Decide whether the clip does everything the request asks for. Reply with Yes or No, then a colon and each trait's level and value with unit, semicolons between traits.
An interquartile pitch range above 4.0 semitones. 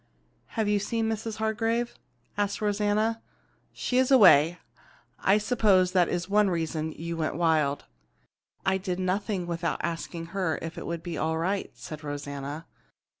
Yes: average, 4.4 semitones